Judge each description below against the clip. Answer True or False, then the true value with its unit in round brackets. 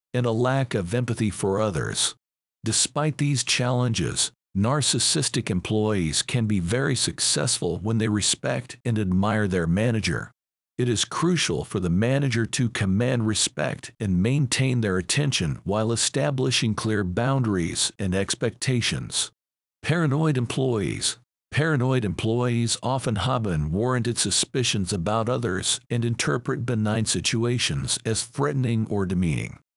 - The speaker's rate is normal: False (120 wpm)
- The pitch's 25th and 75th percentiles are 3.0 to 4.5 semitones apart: True (3.8 semitones)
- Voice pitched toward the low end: True (115 Hz)